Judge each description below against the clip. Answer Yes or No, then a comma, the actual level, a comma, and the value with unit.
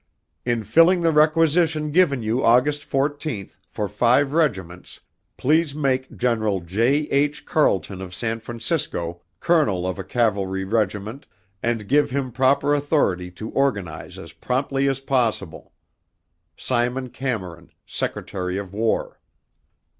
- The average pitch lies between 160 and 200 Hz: No, low, 120 Hz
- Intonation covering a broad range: Yes, wide, 6.4 semitones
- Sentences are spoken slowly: Yes, slow, 125 wpm